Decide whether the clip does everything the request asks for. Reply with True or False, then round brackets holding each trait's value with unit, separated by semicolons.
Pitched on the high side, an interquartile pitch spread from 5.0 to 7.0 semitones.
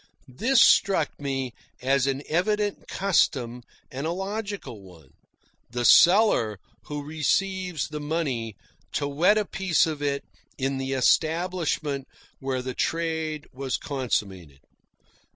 False (145 Hz; 5.3 semitones)